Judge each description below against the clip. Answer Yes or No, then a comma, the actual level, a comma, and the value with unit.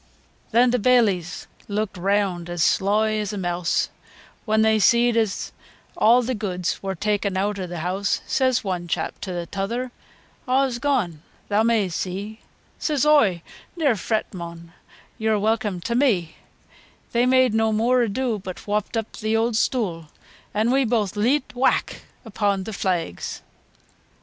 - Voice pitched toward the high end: Yes, high, 215 Hz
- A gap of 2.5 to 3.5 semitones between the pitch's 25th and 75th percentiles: No, average, 4.1 semitones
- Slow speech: No, average, 155 wpm